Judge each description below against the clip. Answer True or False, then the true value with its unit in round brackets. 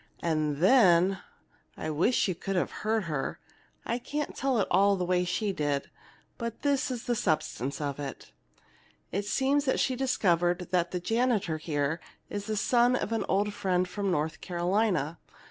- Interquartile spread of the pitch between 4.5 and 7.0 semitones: True (5.5 semitones)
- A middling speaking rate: True (170 wpm)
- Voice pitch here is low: False (185 Hz)